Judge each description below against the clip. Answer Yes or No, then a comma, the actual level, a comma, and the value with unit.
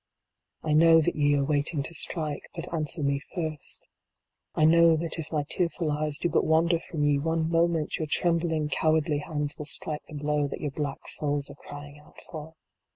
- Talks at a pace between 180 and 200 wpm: Yes, average, 195 wpm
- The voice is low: No, medium, 155 Hz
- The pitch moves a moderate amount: No, narrow, 1.9 semitones